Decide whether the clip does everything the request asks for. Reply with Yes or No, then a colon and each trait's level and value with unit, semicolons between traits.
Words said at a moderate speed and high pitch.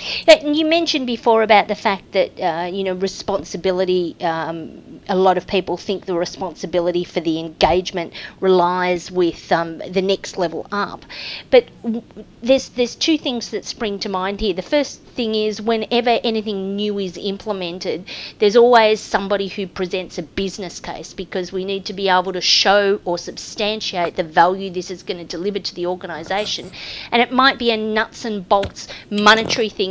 Yes: average, 175 wpm; high, 195 Hz